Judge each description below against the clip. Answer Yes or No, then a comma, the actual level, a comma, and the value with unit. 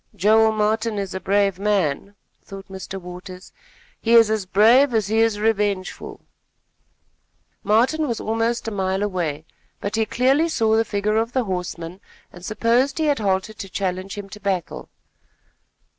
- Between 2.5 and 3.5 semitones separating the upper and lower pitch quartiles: Yes, average, 2.9 semitones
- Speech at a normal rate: Yes, average, 160 wpm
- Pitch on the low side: No, high, 210 Hz